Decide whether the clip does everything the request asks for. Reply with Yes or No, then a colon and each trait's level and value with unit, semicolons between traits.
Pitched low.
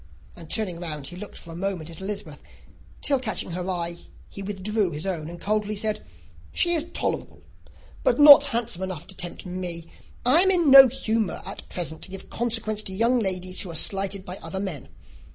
No: high, 195 Hz